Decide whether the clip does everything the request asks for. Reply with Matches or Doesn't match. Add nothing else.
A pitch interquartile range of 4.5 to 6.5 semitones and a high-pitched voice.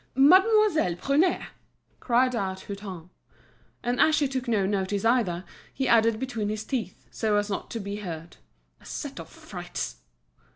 Matches